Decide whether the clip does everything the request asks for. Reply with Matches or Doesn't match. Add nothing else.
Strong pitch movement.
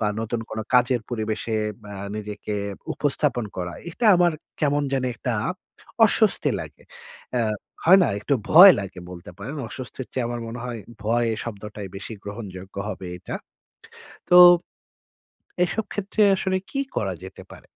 Matches